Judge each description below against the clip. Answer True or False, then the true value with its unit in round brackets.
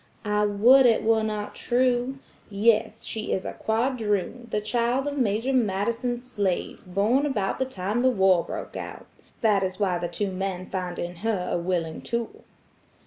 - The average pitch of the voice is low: False (210 Hz)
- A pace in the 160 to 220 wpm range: True (170 wpm)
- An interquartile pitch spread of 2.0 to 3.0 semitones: False (4.0 semitones)